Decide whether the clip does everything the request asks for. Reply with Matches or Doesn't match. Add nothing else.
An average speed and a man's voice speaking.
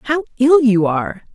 Doesn't match